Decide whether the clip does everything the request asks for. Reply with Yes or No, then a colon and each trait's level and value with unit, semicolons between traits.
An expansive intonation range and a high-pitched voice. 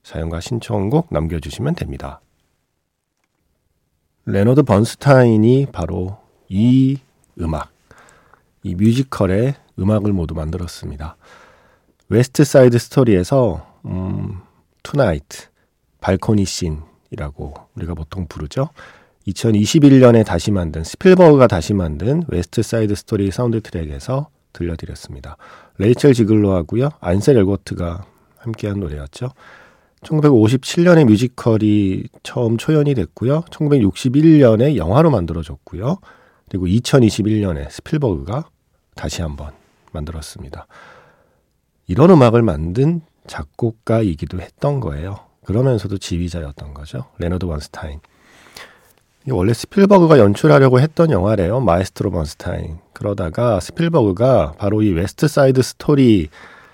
No: wide, 7.0 semitones; low, 105 Hz